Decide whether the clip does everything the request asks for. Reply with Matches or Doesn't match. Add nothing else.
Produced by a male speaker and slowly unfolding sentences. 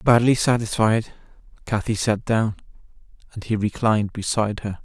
Matches